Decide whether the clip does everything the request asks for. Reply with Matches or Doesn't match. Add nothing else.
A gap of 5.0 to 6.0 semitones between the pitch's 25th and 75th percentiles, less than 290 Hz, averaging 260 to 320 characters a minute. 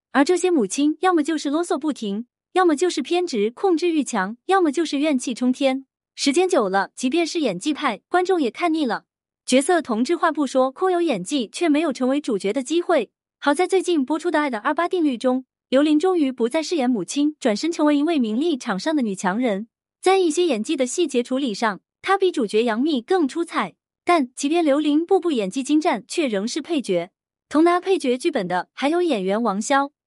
Doesn't match